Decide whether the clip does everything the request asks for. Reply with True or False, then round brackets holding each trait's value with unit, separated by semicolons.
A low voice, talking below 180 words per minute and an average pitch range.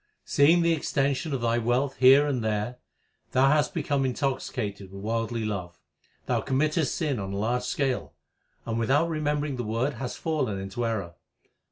True (125 Hz; 170 wpm; 4.4 semitones)